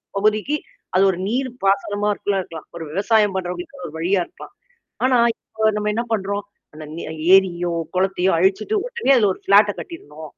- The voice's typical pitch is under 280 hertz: Yes, high, 195 Hz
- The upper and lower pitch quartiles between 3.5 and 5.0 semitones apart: No, average, 3.1 semitones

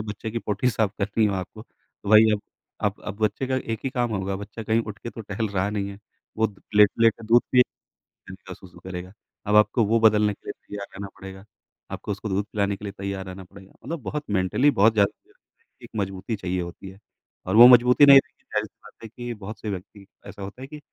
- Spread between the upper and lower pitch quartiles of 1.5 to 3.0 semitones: Yes, narrow, 2.5 semitones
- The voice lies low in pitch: Yes, low, 105 Hz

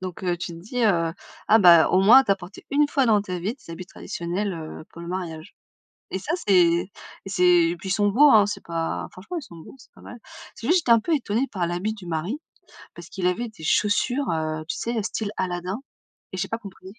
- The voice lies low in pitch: No, high, 190 Hz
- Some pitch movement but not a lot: Yes, average, 4.4 semitones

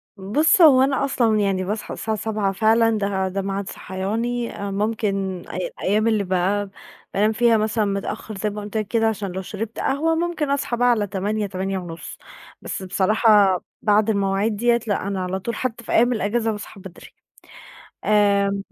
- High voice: Yes, high, 210 Hz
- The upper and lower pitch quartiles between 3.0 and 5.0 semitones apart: No, narrow, 2.6 semitones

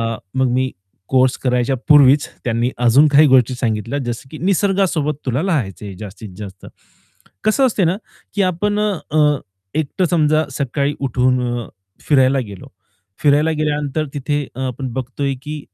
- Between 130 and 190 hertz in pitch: Yes, medium, 140 Hz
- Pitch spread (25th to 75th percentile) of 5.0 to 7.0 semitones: No, average, 3.6 semitones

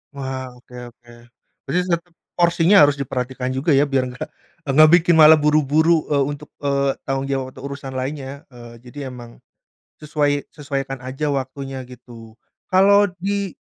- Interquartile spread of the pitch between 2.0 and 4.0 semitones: Yes, average, 2.8 semitones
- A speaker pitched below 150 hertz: Yes, medium, 140 Hz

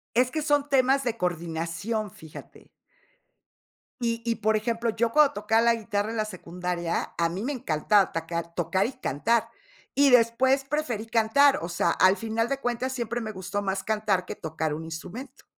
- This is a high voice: Yes, high, 220 Hz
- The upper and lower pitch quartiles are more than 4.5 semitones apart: Yes, average, 5.0 semitones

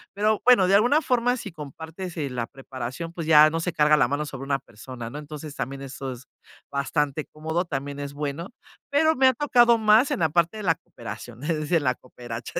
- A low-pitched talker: No, medium, 155 Hz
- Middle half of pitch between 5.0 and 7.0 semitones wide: Yes, wide, 5.6 semitones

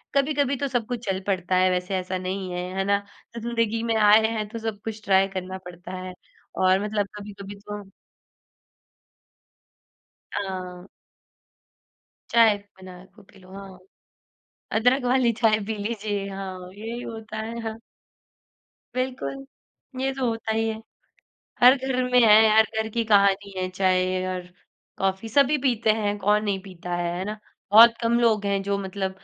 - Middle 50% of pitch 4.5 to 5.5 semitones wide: No, average, 3.2 semitones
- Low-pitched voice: No, high, 205 Hz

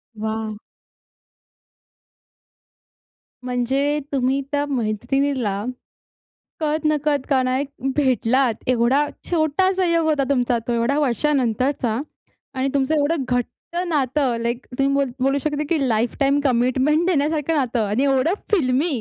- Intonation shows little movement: No, average, 3.2 semitones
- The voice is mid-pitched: No, very high, 270 Hz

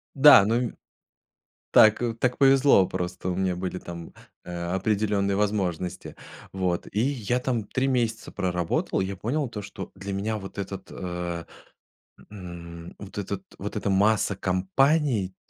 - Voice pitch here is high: No, low, 100 Hz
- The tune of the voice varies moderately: Yes, average, 3.7 semitones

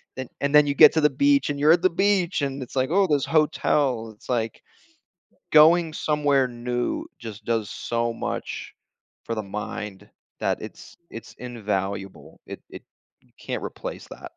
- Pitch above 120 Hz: Yes, low, 135 Hz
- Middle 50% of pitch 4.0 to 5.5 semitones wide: Yes, average, 5.0 semitones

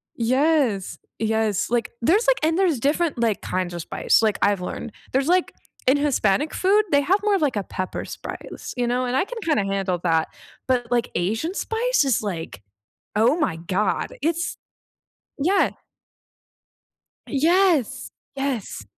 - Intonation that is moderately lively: No, wide, 7.6 semitones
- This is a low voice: No, very high, 255 Hz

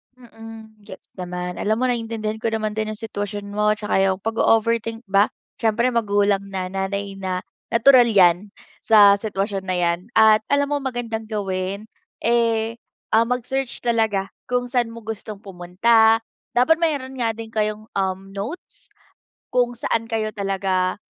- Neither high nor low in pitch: No, high, 220 Hz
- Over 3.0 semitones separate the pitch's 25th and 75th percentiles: No, average, 2.7 semitones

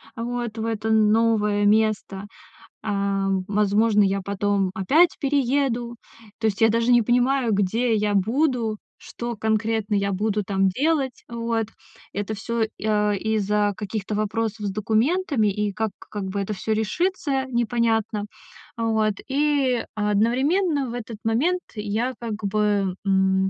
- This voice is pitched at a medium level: No, high, 220 Hz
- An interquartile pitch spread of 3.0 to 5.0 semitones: No, narrow, 2.6 semitones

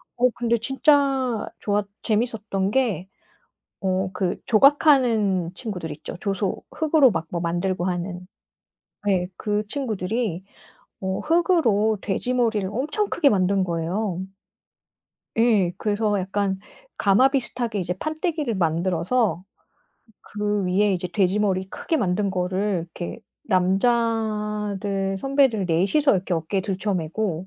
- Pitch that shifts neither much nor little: Yes, average, 4.2 semitones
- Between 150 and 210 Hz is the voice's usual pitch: Yes, high, 205 Hz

